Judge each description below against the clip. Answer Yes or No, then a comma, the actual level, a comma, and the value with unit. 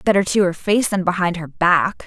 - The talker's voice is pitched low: No, medium, 180 Hz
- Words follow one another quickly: Yes, fast, 235 wpm